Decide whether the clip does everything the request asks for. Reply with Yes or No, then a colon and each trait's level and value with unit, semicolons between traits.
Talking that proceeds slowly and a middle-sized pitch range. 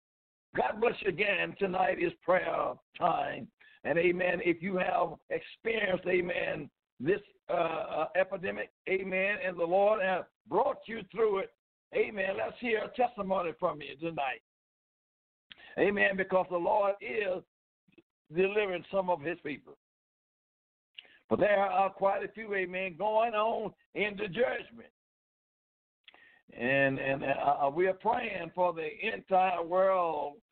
Yes: slow, 130 wpm; average, 3.2 semitones